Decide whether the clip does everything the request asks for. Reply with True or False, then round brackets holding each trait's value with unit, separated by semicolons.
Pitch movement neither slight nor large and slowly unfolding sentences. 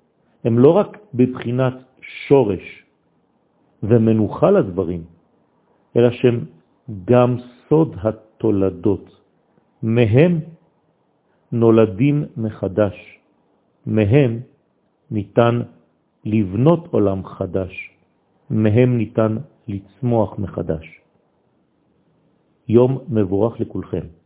True (3.9 semitones; 65 wpm)